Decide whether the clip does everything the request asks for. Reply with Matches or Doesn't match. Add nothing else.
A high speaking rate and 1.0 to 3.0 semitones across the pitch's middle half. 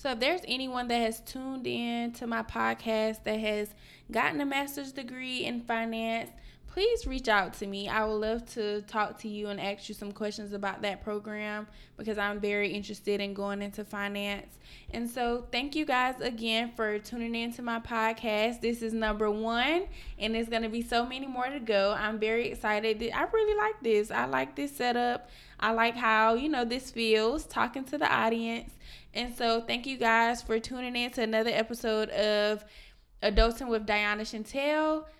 Doesn't match